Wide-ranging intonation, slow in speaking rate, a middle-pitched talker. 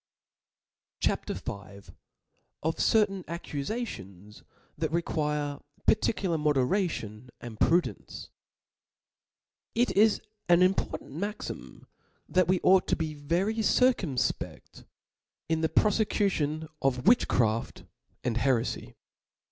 Yes: wide, 6.8 semitones; slow, 100 wpm; medium, 160 Hz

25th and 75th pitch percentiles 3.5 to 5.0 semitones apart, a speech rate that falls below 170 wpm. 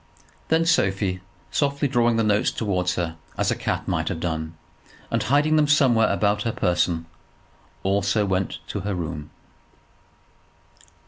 No: wide, 5.6 semitones; average, 140 wpm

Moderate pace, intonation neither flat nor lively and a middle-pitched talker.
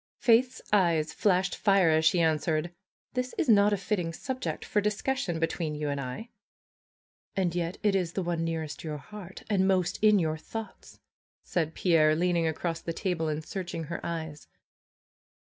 Yes: average, 165 wpm; average, 3.8 semitones; medium, 175 Hz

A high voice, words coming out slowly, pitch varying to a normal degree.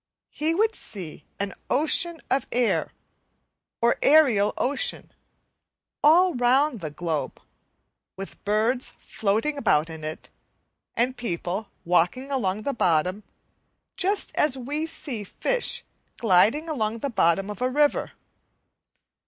No: high, 240 Hz; slow, 120 wpm; wide, 7.1 semitones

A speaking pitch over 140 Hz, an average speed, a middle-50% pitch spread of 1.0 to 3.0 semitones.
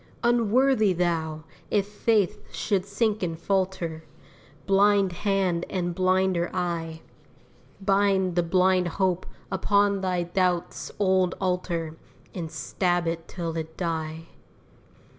No: medium, 185 Hz; slow, 110 wpm; narrow, 2.5 semitones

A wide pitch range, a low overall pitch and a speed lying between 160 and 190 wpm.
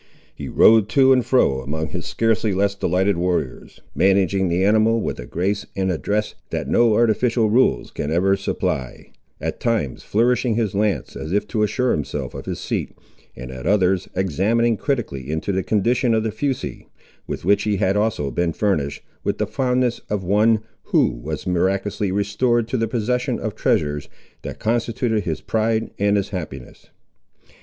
No: average, 3.8 semitones; low, 105 Hz; average, 170 wpm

